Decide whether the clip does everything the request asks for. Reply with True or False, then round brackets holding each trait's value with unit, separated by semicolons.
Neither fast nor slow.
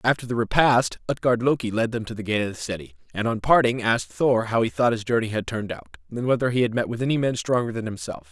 False (265 wpm)